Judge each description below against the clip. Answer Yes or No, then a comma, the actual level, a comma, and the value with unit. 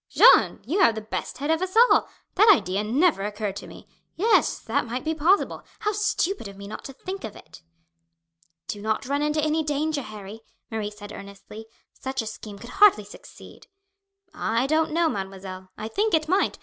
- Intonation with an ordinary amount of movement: No, wide, 7.5 semitones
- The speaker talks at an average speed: Yes, average, 190 wpm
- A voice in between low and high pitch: No, very high, 260 Hz